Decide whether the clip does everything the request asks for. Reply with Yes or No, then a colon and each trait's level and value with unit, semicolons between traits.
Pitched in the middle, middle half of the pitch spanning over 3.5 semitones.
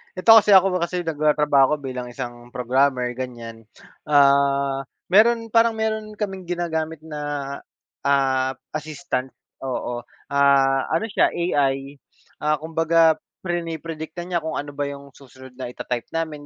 Yes: medium, 145 Hz; average, 4.0 semitones